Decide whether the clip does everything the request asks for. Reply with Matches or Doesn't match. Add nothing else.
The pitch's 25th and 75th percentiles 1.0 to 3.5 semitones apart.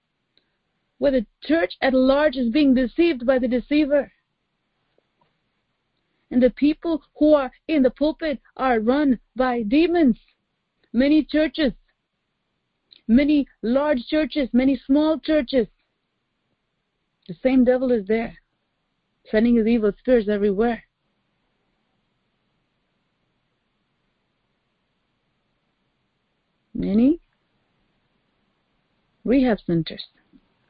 Doesn't match